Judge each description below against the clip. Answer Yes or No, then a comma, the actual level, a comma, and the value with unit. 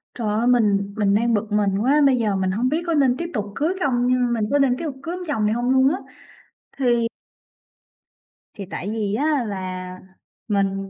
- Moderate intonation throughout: Yes, average, 4.4 semitones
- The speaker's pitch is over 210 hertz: Yes, high, 235 Hz